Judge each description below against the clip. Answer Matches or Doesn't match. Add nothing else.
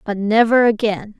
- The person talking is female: Matches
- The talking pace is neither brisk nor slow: Matches